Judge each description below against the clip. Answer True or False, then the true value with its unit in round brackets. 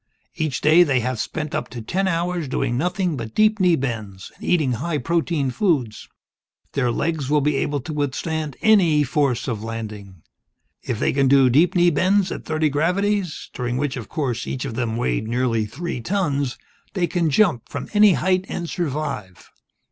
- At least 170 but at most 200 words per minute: True (180 wpm)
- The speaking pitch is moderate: True (145 Hz)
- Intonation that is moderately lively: False (5.8 semitones)